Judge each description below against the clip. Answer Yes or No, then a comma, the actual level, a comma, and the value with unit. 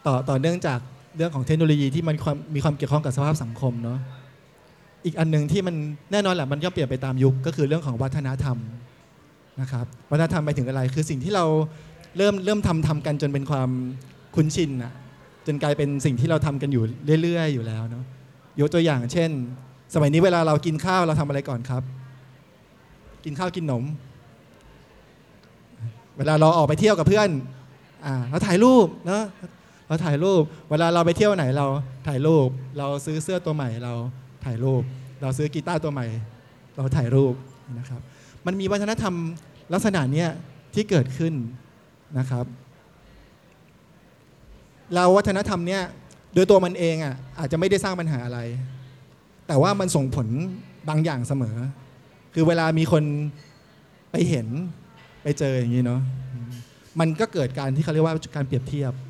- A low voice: No, medium, 145 Hz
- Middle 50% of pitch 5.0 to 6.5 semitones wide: No, average, 3.9 semitones